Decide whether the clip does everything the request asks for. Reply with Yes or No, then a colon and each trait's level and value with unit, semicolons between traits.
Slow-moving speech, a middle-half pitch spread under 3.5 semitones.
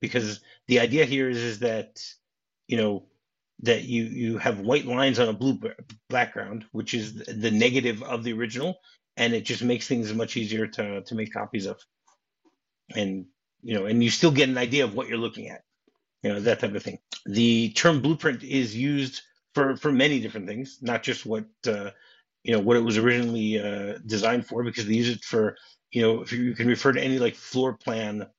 No: fast, 205 wpm; average, 2.8 semitones